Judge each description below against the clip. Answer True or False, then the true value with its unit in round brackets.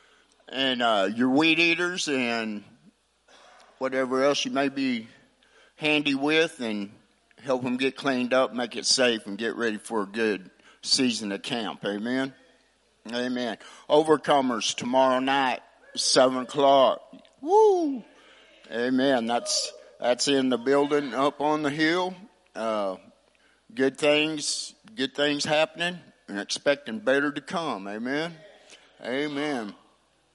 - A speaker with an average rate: False (125 wpm)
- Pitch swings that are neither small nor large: True (3.7 semitones)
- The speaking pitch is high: False (135 Hz)